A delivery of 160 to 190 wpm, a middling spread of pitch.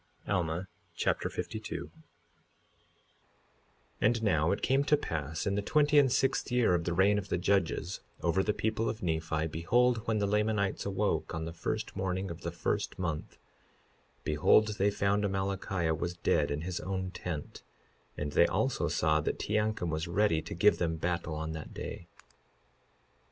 Yes: average, 165 wpm; average, 4.3 semitones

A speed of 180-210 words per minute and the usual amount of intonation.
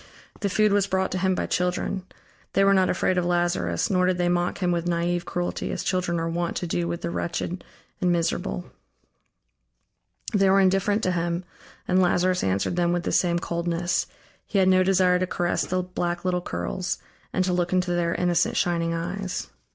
No: average, 195 wpm; narrow, 1.2 semitones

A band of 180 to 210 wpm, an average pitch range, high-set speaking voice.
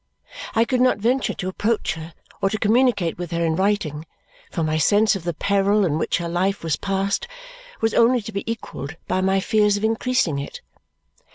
Yes: average, 195 wpm; average, 4.6 semitones; high, 195 Hz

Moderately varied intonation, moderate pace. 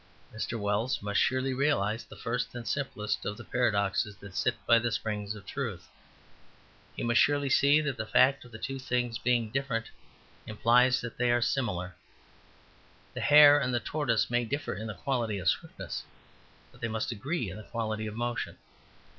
Yes: average, 3.3 semitones; average, 180 wpm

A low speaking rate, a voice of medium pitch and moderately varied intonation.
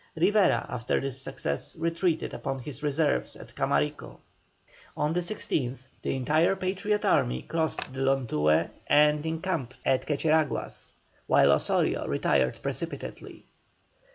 Yes: slow, 120 wpm; medium, 150 Hz; average, 4.4 semitones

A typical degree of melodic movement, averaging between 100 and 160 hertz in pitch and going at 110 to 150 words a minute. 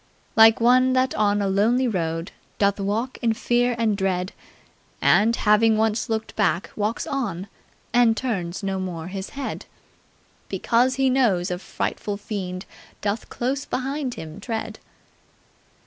No: average, 4.1 semitones; high, 215 Hz; average, 140 wpm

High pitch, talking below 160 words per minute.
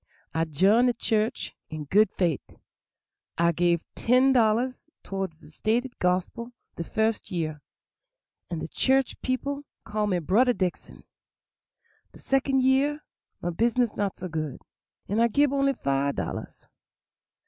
Yes: high, 215 Hz; slow, 135 wpm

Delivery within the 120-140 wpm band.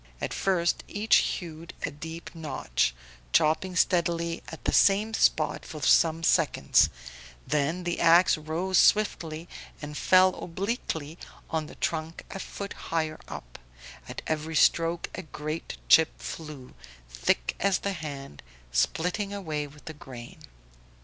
Yes: slow, 135 wpm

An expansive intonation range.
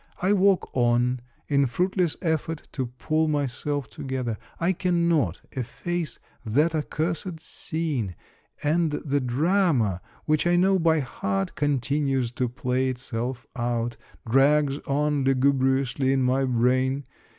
No: average, 4.1 semitones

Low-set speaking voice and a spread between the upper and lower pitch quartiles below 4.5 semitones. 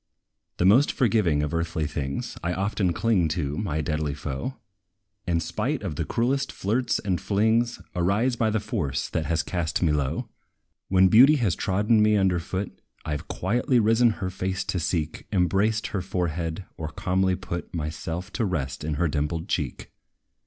No: very low, 90 Hz; average, 5.0 semitones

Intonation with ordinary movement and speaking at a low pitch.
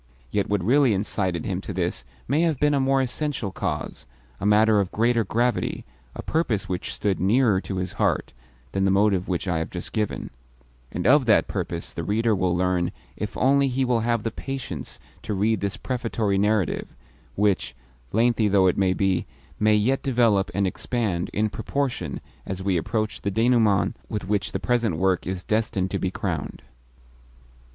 Yes: average, 4.1 semitones; low, 105 Hz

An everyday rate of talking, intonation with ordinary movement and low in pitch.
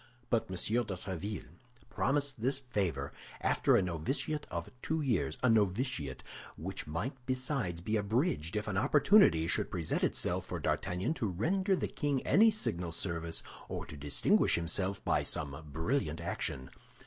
No: average, 150 wpm; wide, 7.8 semitones; low, 100 Hz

